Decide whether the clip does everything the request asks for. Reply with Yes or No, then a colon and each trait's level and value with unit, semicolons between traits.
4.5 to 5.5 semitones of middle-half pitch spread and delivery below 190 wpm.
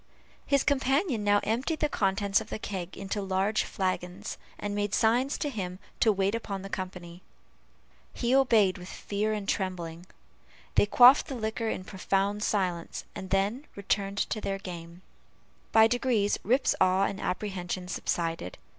No: average, 3.0 semitones; average, 155 wpm